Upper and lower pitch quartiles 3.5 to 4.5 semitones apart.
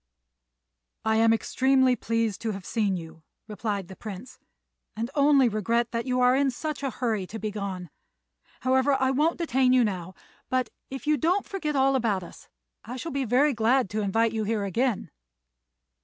Yes: average, 3.8 semitones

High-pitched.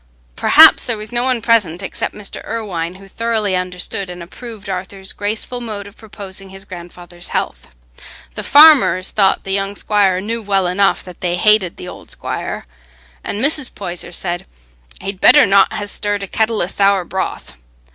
Yes: high, 195 Hz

